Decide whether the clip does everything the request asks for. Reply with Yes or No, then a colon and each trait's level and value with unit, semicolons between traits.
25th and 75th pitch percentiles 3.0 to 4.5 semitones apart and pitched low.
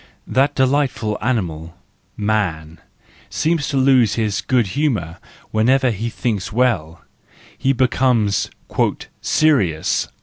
No: average, 5.2 semitones; low, 115 Hz